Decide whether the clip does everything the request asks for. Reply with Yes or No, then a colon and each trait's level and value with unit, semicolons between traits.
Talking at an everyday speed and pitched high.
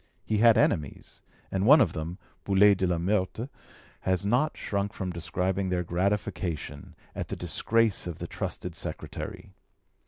No: average, 150 wpm; very low, 95 Hz